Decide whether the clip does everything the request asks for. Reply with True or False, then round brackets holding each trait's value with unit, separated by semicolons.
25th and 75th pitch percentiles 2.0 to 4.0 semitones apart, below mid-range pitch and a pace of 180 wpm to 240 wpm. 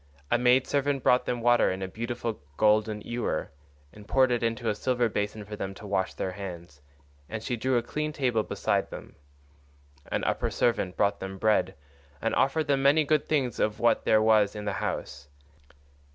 True (3.4 semitones; 115 Hz; 190 wpm)